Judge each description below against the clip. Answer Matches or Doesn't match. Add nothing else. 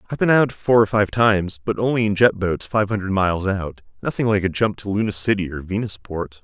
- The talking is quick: Matches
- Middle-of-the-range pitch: Doesn't match